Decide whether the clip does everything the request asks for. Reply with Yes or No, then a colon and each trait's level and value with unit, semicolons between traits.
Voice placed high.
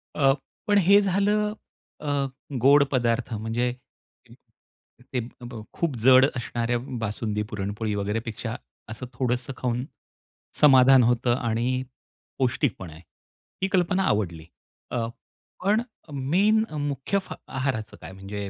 No: low, 125 Hz